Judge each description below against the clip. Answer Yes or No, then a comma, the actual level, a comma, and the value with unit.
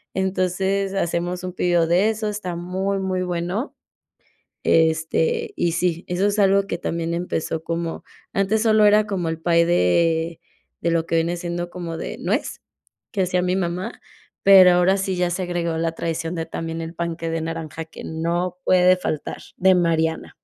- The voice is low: No, medium, 175 Hz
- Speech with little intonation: Yes, narrow, 2.2 semitones